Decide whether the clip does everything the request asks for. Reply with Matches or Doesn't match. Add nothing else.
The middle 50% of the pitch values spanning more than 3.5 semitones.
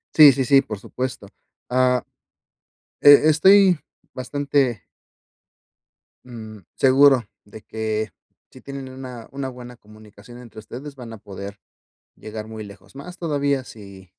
Matches